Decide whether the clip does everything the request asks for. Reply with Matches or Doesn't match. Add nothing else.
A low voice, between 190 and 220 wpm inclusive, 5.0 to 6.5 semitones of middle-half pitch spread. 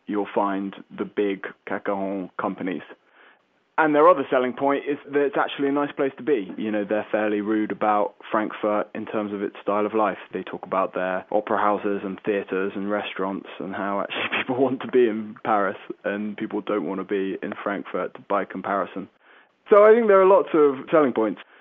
Matches